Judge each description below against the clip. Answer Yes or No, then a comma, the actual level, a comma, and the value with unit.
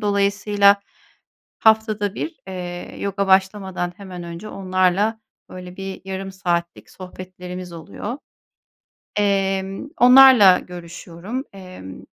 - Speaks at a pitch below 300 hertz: Yes, high, 190 Hz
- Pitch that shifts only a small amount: Yes, narrow, 2.1 semitones